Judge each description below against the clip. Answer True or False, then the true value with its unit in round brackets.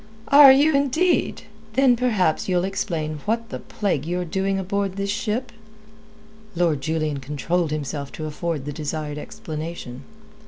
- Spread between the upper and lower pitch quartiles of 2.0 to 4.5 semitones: False (5.6 semitones)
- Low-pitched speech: False (175 Hz)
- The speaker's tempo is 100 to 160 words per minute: True (135 wpm)